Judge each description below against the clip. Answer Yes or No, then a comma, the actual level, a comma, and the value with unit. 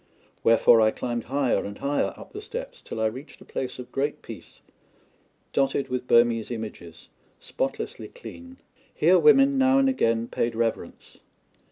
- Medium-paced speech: Yes, average, 155 wpm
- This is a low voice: Yes, low, 130 Hz